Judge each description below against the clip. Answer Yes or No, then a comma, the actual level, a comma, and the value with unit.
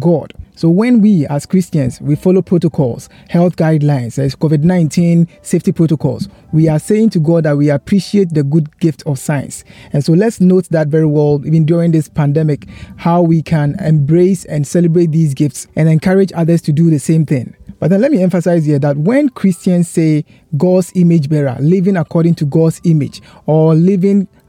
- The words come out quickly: No, average, 185 wpm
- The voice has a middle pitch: Yes, medium, 165 Hz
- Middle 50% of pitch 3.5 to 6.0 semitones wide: No, average, 3.0 semitones